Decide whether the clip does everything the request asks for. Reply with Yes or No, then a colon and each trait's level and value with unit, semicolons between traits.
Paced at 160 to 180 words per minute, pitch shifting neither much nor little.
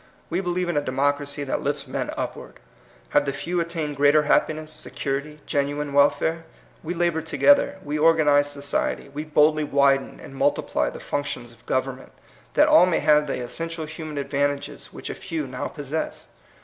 No: average, 170 wpm; narrow, 2.2 semitones